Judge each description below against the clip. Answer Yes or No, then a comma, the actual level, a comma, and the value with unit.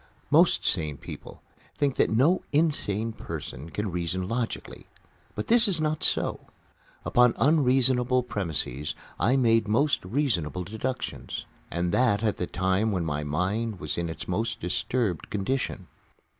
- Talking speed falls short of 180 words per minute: Yes, average, 140 wpm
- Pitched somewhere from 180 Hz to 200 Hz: No, low, 110 Hz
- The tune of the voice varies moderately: No, wide, 6.2 semitones